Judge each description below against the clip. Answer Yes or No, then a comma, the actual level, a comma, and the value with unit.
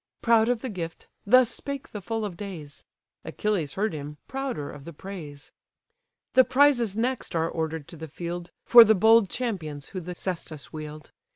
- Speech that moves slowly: No, average, 175 wpm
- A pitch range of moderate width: No, wide, 6.4 semitones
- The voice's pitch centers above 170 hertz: Yes, high, 190 Hz